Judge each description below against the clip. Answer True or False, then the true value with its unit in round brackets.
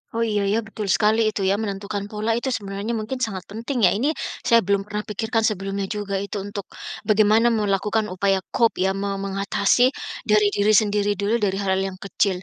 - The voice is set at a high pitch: True (205 Hz)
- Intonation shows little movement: True (1.7 semitones)